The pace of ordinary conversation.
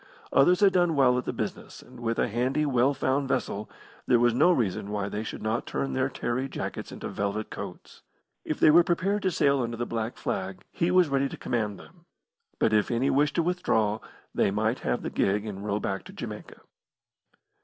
No: fast, 210 wpm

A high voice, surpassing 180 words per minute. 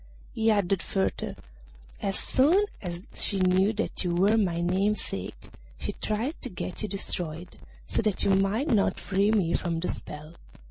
No: high, 195 Hz; average, 165 wpm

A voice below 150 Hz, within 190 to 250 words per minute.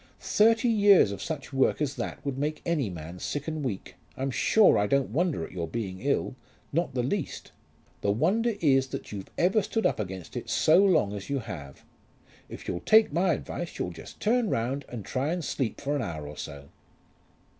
Yes: low, 135 Hz; average, 200 wpm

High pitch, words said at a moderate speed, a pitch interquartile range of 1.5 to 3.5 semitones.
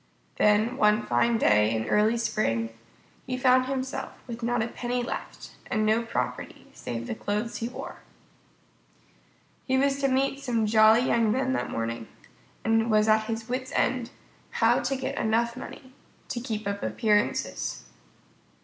Yes: high, 230 Hz; average, 160 wpm; average, 3.1 semitones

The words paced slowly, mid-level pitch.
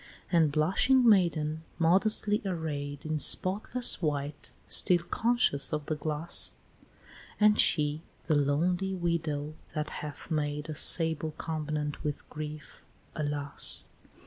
Yes: slow, 115 wpm; medium, 155 Hz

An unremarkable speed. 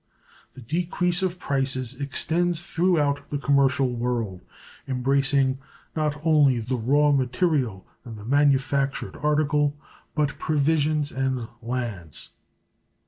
No: slow, 105 wpm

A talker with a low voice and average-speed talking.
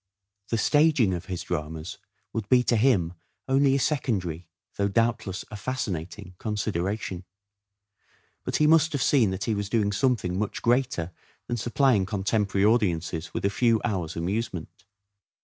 Yes: low, 105 Hz; average, 150 wpm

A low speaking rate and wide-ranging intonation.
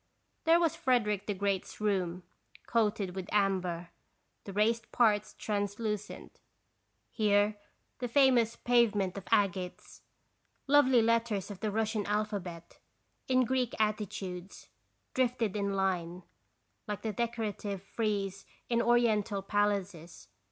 No: slow, 110 wpm; average, 2.9 semitones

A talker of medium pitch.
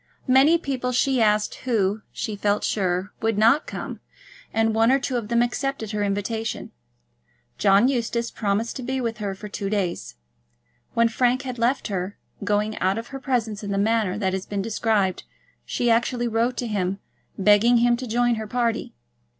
No: high, 225 Hz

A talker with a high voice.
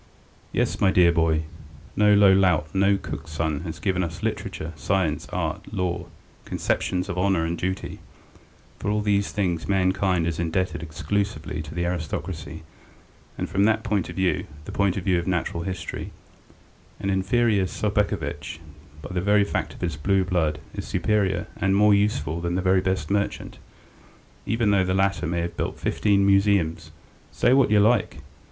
No: very low, 95 Hz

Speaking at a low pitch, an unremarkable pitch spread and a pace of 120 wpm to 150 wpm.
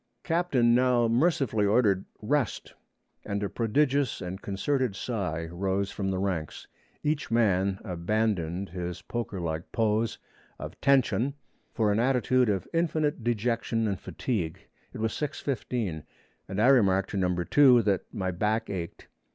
Yes: low, 110 Hz; average, 4.8 semitones; average, 140 wpm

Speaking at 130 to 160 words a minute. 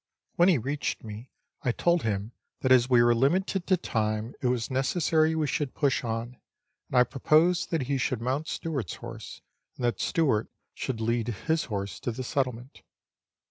No: average, 180 wpm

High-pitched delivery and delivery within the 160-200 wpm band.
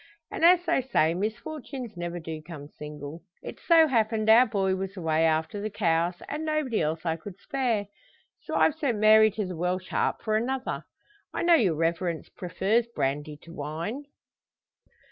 Yes: high, 195 Hz; average, 170 wpm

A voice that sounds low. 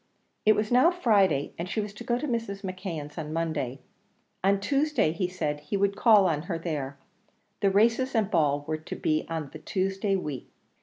No: high, 190 Hz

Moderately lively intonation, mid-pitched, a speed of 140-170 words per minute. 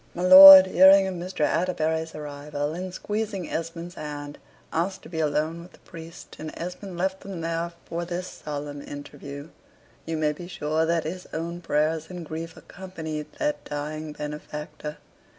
Yes: average, 3.1 semitones; medium, 165 Hz; average, 160 wpm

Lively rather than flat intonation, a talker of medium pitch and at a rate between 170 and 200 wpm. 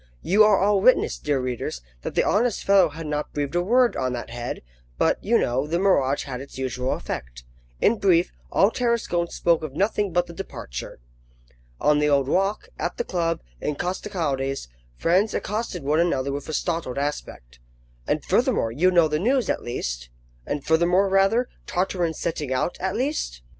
Yes: wide, 6.1 semitones; medium, 165 Hz; average, 180 wpm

